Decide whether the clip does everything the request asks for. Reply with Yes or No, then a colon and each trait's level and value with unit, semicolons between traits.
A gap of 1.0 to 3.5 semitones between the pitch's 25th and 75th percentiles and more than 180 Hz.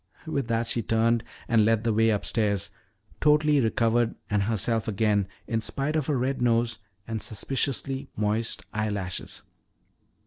No: average, 2.8 semitones; low, 115 Hz